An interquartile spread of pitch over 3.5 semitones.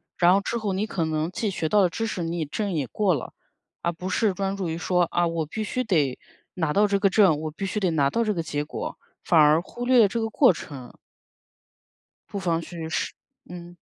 Yes: average, 4.2 semitones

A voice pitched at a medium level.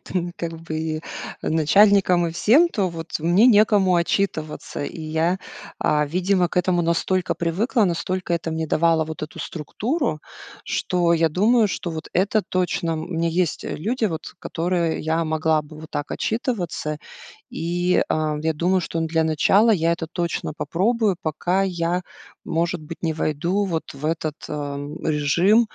Yes: medium, 170 Hz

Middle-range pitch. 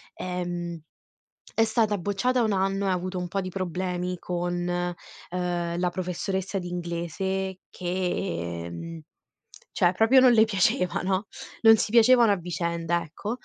Yes: medium, 180 Hz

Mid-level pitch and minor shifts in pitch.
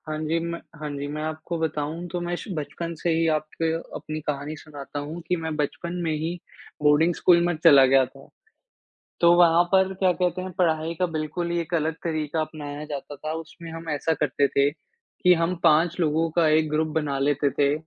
Yes: medium, 155 Hz; narrow, 2.3 semitones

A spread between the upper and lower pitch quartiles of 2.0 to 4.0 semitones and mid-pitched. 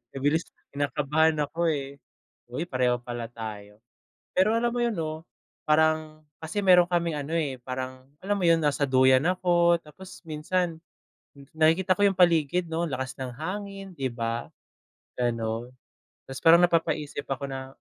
No: average, 4.8 semitones; medium, 155 Hz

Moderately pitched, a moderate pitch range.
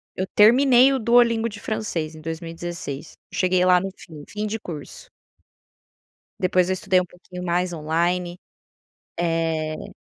Yes: medium, 180 Hz; average, 4.0 semitones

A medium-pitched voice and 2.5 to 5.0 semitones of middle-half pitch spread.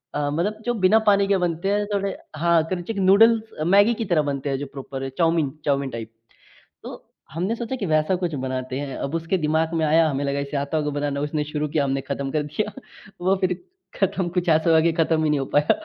Yes: medium, 160 Hz; average, 4.6 semitones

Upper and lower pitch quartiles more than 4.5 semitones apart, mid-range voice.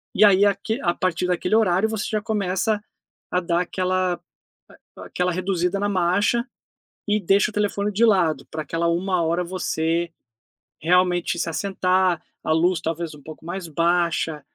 No: average, 2.8 semitones; medium, 180 Hz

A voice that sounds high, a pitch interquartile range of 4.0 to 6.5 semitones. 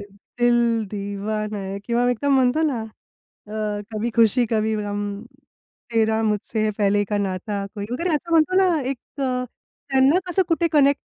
Yes: high, 225 Hz; average, 4.6 semitones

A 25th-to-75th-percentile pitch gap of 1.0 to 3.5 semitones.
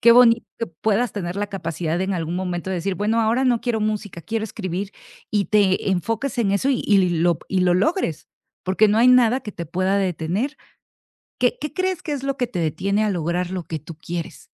No: average, 4.7 semitones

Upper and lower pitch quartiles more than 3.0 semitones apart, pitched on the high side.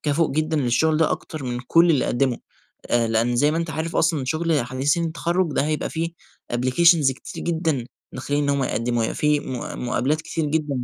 No: average, 4.0 semitones; medium, 150 Hz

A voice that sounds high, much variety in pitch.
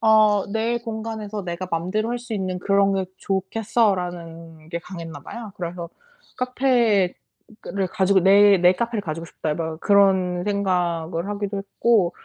No: high, 195 Hz; average, 3.6 semitones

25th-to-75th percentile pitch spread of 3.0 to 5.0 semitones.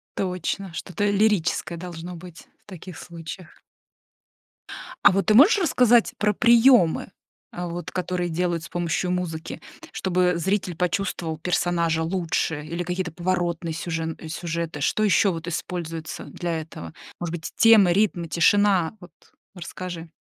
No: narrow, 2.4 semitones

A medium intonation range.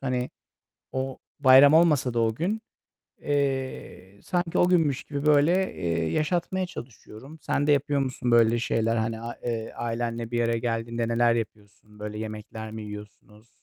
Yes: average, 4.3 semitones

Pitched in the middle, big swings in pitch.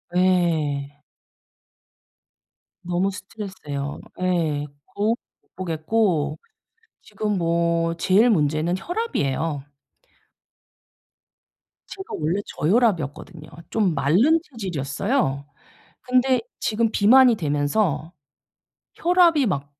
Yes: medium, 175 Hz; wide, 6.5 semitones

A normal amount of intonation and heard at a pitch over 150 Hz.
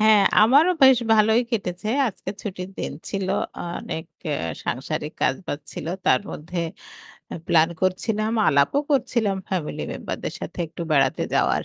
No: wide, 5.7 semitones; high, 190 Hz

